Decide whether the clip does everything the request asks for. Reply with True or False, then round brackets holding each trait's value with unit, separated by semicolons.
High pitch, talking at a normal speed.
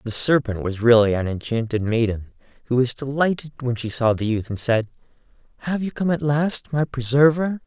False (125 Hz; 190 wpm)